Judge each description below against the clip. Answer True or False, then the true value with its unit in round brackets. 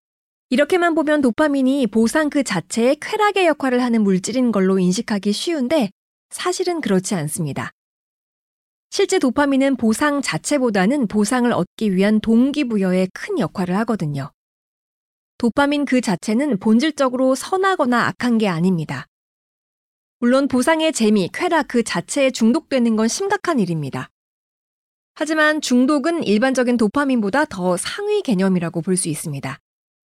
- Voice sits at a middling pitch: False (245 Hz)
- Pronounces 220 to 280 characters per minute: False (310 characters per minute)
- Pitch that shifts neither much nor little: False (6.8 semitones)